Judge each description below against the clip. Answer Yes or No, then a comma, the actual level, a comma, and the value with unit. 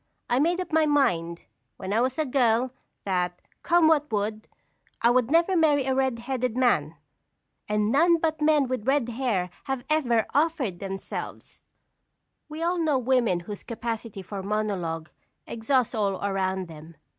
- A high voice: Yes, high, 240 Hz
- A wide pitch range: Yes, wide, 6.3 semitones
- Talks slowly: No, average, 155 wpm